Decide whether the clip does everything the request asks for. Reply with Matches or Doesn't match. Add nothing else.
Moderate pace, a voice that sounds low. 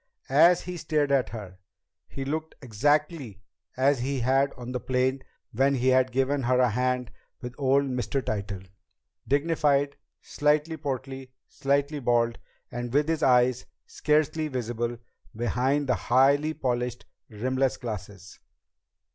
Doesn't match